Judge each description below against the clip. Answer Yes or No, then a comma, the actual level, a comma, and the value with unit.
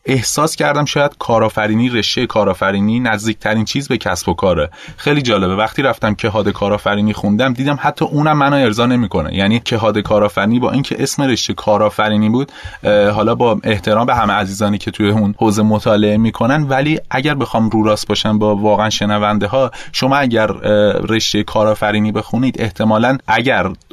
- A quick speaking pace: Yes, fast, 160 wpm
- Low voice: Yes, low, 110 Hz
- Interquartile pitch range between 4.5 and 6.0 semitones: No, average, 3.2 semitones